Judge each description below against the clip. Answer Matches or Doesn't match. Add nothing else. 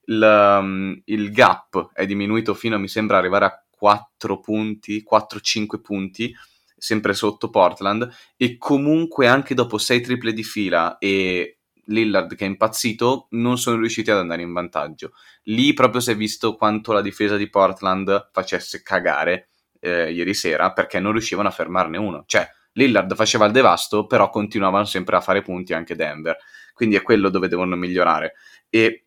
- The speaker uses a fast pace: Doesn't match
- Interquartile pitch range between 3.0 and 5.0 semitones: Doesn't match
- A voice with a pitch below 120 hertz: Matches